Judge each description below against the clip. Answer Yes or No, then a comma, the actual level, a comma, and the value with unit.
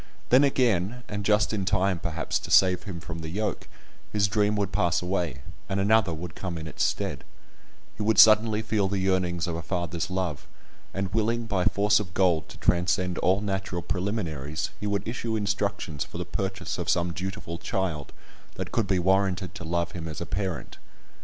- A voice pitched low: Yes, very low, 95 Hz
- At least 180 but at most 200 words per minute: Yes, average, 190 wpm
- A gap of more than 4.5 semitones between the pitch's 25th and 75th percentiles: No, average, 3.0 semitones